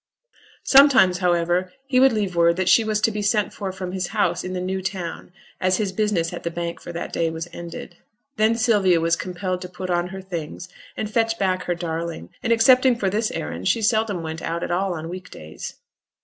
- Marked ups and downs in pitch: No, average, 3.6 semitones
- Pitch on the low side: No, medium, 185 Hz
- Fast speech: Yes, fast, 220 wpm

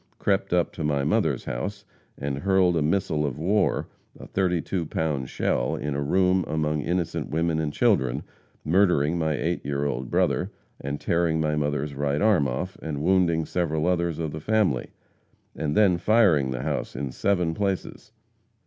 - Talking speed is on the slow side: No, average, 165 wpm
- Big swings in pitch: No, average, 3.9 semitones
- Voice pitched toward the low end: Yes, very low, 80 Hz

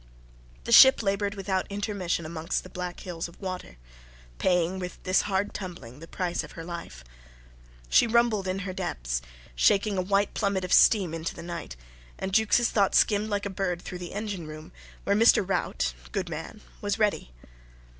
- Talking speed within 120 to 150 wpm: No, average, 175 wpm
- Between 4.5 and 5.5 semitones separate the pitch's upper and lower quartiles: No, average, 2.9 semitones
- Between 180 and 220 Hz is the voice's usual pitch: Yes, medium, 185 Hz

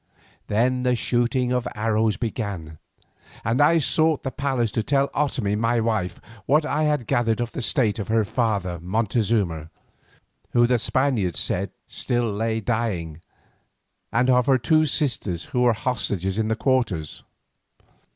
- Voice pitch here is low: Yes, low, 115 Hz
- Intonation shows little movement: No, average, 3.4 semitones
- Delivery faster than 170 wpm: No, average, 150 wpm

